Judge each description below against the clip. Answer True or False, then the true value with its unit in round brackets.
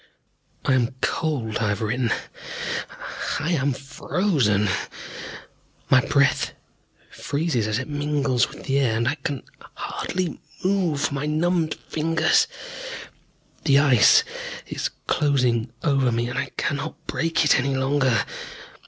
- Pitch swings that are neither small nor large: True (4.1 semitones)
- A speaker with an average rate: False (125 wpm)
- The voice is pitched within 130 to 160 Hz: True (140 Hz)